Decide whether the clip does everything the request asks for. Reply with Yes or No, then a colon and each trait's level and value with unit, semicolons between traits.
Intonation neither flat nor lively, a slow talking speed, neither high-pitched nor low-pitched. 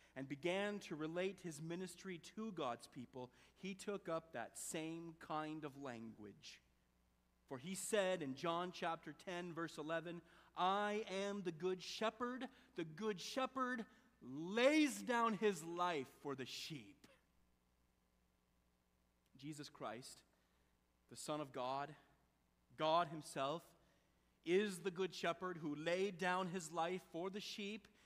No: wide, 6.4 semitones; slow, 130 wpm; medium, 165 Hz